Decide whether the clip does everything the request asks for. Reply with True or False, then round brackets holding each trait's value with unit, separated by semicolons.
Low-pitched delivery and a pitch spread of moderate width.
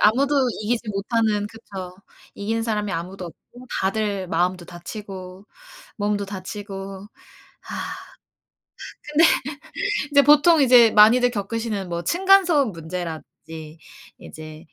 False (205 Hz; 4.2 semitones)